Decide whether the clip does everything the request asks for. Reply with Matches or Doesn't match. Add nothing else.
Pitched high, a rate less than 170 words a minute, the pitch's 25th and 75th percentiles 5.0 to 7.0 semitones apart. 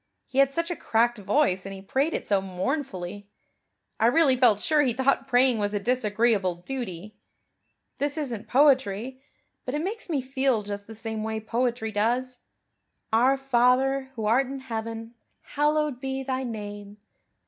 Doesn't match